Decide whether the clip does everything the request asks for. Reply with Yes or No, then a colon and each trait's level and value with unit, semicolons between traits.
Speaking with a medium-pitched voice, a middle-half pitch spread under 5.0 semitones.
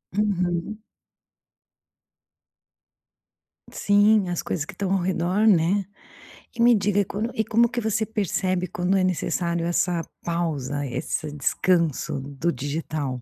Yes: medium, 180 Hz; average, 3.9 semitones